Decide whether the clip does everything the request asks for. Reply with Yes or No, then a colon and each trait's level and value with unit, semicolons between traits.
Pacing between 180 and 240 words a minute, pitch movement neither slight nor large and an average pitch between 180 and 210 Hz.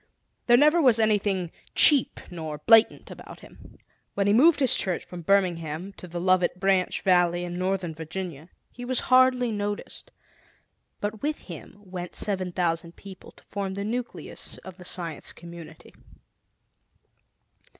No: average, 145 wpm; average, 3.7 semitones; high, 190 Hz